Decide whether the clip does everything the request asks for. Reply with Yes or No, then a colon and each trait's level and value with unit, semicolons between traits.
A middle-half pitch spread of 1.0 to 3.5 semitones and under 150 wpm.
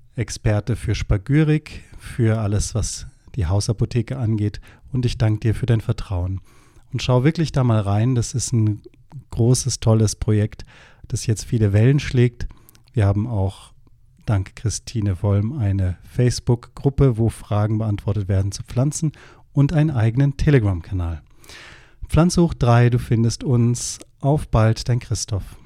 Yes: average, 3.2 semitones; average, 140 wpm